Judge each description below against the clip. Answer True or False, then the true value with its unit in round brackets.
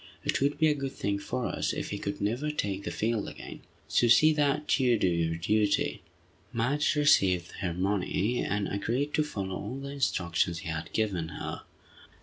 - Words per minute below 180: False (185 wpm)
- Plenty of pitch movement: True (6.5 semitones)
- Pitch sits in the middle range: False (105 Hz)